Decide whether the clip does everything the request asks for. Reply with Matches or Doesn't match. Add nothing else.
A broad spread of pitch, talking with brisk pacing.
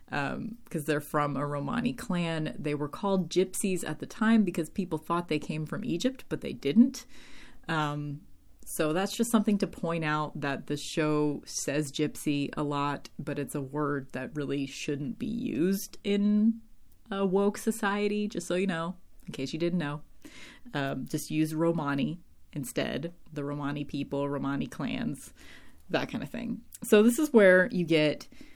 Doesn't match